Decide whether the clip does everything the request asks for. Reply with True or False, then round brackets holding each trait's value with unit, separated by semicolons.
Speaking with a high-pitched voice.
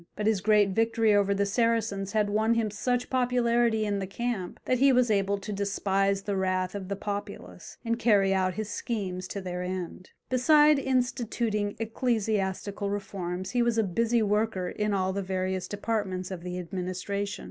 True (205 Hz)